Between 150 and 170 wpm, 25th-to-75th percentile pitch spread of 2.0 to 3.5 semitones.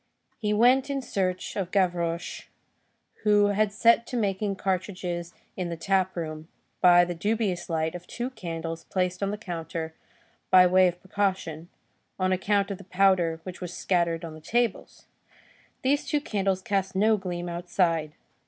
Yes: average, 160 wpm; average, 2.8 semitones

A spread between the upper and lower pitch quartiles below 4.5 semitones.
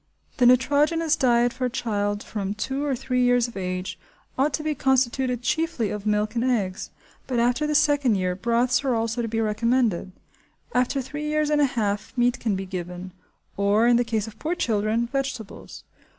Yes: average, 4.0 semitones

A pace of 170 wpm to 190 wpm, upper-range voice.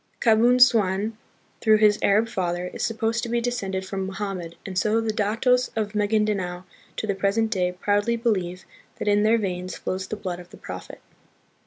Yes: average, 180 wpm; high, 205 Hz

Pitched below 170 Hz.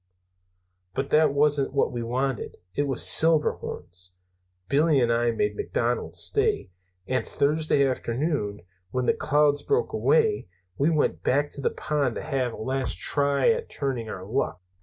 Yes: medium, 140 Hz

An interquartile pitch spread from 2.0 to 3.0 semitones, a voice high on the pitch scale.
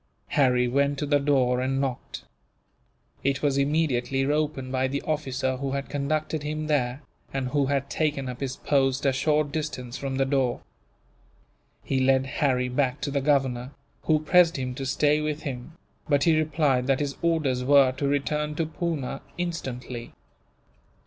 No: narrow, 2.4 semitones; medium, 140 Hz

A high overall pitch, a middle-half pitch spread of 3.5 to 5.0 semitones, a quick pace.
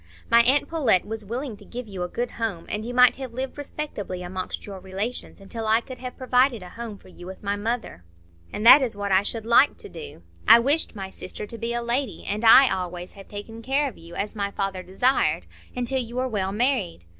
Yes: high, 225 Hz; average, 4.3 semitones; fast, 230 wpm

